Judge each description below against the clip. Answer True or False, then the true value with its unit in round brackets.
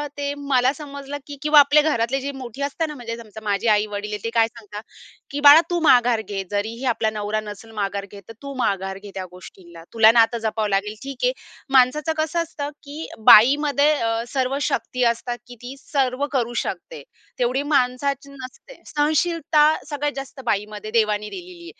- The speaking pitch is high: True (250 Hz)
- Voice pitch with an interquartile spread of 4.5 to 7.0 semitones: True (5.0 semitones)